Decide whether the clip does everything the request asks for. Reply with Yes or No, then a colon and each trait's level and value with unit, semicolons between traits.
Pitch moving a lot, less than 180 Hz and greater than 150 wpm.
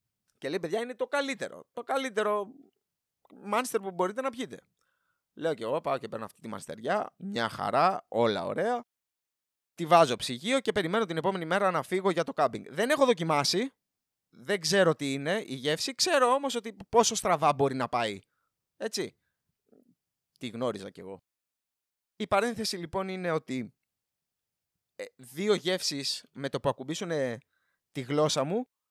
No: wide, 8.2 semitones; high, 195 Hz; average, 160 wpm